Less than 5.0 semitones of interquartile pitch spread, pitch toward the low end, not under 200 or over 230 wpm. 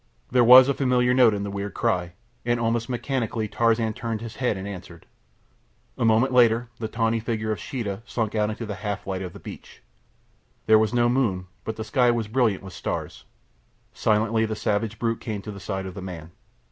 Yes: average, 2.7 semitones; low, 110 Hz; fast, 205 wpm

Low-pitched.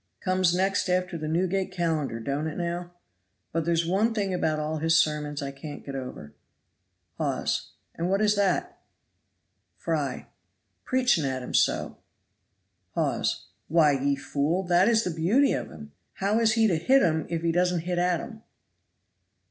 No: medium, 170 Hz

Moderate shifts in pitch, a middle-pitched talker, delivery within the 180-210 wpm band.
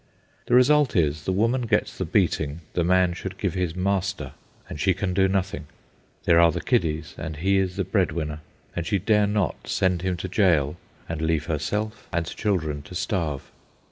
No: average, 3.5 semitones; very low, 90 Hz; average, 190 wpm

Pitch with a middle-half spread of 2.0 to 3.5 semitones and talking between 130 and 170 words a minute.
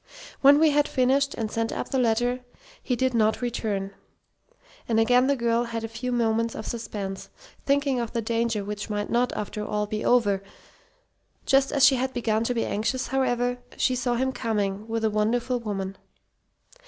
No: narrow, 2.6 semitones; average, 180 wpm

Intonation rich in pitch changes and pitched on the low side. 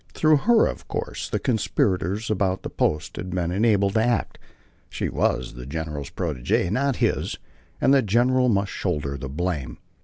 Yes: wide, 7.1 semitones; very low, 95 Hz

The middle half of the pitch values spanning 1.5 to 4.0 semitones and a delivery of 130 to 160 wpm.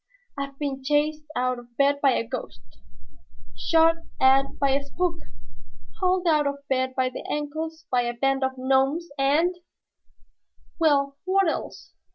Yes: average, 3.1 semitones; average, 155 wpm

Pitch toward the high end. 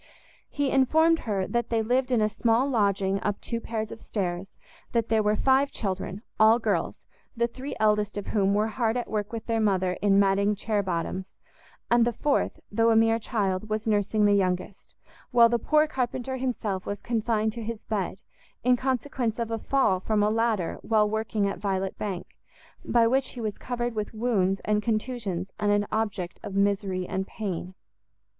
Yes: high, 215 Hz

